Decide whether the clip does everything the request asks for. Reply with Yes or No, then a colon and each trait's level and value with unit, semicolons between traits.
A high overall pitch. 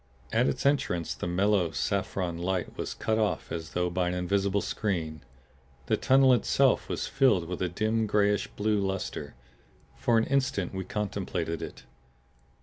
No: low, 100 Hz